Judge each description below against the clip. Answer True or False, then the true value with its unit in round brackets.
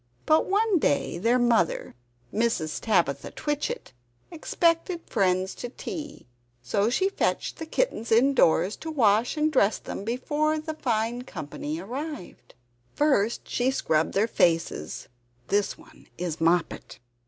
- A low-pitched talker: False (235 Hz)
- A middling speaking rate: False (130 wpm)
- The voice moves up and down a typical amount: False (8.6 semitones)